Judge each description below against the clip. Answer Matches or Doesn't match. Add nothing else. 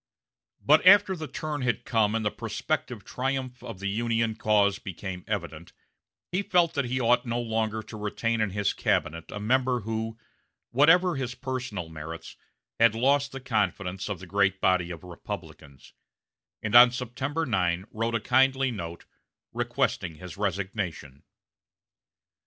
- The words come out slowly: Doesn't match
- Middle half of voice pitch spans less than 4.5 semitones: Doesn't match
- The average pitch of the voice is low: Matches